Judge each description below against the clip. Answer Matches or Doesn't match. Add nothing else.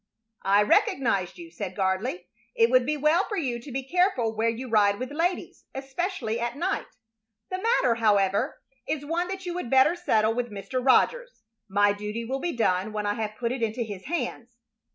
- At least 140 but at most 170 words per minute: Doesn't match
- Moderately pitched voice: Doesn't match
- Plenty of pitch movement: Matches